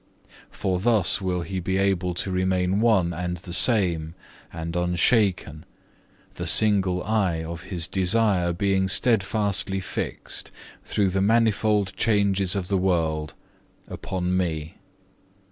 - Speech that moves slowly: Yes, slow, 125 wpm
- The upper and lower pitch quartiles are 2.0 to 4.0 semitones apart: Yes, narrow, 2.4 semitones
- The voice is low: Yes, very low, 95 Hz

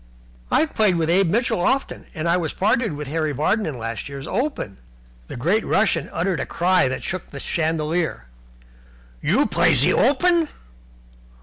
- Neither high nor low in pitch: Yes, medium, 170 Hz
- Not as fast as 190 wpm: Yes, average, 170 wpm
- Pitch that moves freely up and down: Yes, wide, 5.8 semitones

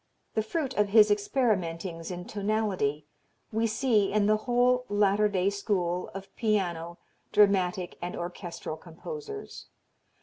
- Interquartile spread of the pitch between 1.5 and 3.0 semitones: No, average, 3.5 semitones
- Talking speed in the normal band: No, slow, 125 wpm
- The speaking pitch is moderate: No, high, 205 Hz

